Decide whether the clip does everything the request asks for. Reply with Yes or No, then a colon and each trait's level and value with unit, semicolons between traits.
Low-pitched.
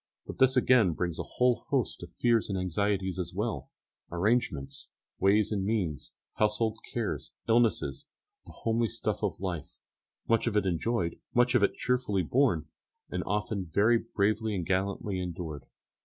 Yes: low, 100 Hz